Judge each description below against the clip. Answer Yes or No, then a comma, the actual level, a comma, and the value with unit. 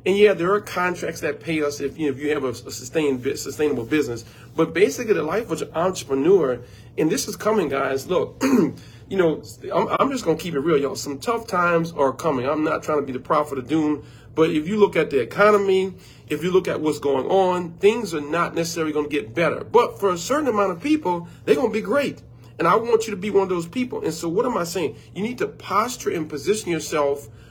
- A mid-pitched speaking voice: Yes, medium, 160 Hz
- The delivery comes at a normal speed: No, fast, 245 wpm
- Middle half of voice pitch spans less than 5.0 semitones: No, wide, 5.5 semitones